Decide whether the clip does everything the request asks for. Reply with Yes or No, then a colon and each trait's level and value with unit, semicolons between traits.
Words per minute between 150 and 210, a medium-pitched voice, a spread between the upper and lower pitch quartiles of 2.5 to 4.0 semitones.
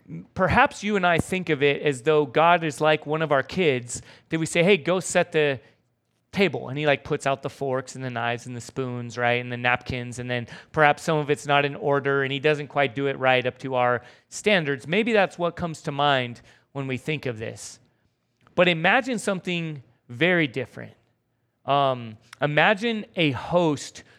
No: average, 200 wpm; medium, 145 Hz; average, 4.7 semitones